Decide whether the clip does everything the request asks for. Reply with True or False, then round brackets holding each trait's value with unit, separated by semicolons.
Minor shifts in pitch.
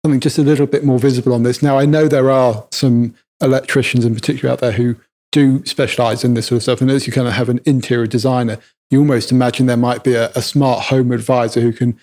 True (2.0 semitones)